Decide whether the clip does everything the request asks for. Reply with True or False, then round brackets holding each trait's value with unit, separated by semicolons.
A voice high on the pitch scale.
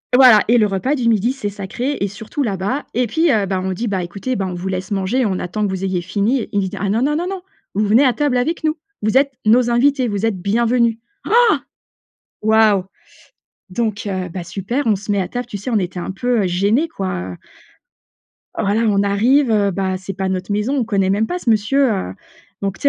True (210 Hz)